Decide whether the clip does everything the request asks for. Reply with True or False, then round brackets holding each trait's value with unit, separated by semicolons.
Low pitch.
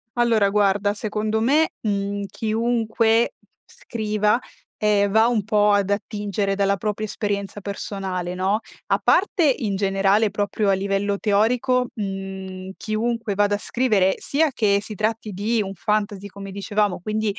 False (205 Hz)